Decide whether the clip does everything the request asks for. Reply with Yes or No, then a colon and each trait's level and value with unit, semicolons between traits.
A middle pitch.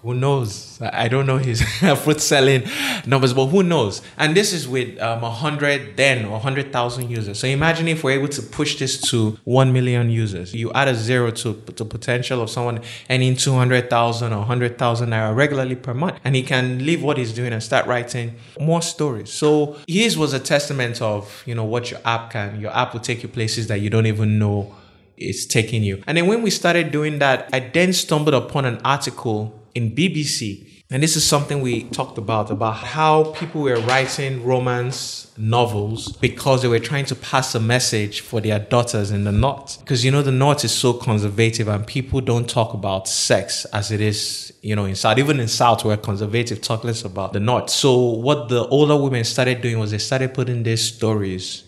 No: low, 125 Hz